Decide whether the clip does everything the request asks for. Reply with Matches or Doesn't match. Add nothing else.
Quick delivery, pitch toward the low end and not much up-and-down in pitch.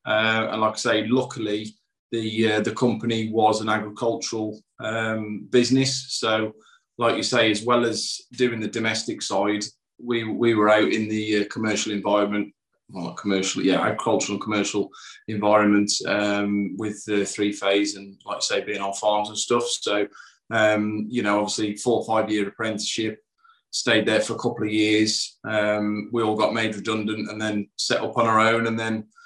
Doesn't match